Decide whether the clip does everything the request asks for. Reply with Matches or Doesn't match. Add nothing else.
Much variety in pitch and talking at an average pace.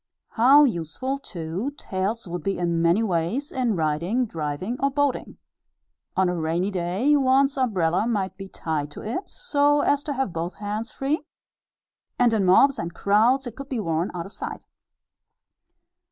Matches